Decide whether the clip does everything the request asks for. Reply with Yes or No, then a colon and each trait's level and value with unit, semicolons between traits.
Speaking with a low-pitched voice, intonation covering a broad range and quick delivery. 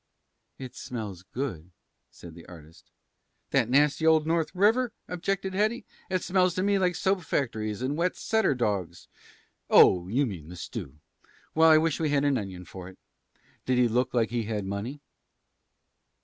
No: low, 130 Hz; wide, 9.0 semitones; average, 165 wpm